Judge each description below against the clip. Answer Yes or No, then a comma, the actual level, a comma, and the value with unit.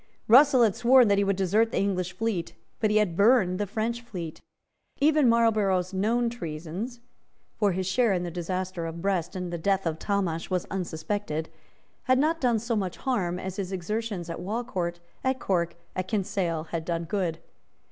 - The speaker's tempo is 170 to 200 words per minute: Yes, average, 190 wpm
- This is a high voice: Yes, high, 195 Hz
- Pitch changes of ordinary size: Yes, average, 4.5 semitones